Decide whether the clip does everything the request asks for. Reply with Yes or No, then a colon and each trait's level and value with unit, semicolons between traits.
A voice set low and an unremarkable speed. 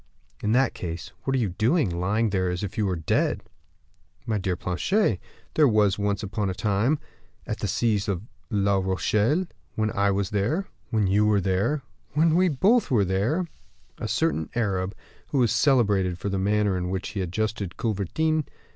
Yes: low, 105 Hz; average, 180 wpm